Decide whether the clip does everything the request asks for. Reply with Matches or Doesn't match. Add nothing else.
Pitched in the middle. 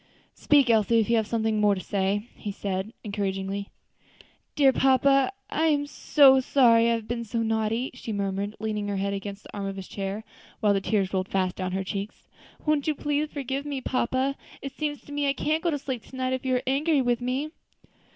Doesn't match